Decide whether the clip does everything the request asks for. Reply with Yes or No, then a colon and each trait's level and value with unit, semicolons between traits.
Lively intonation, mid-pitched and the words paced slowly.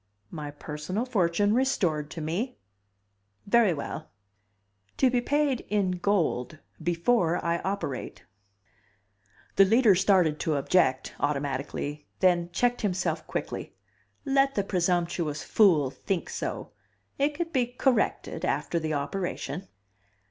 Yes: wide, 6.3 semitones; medium, 175 Hz; slow, 120 wpm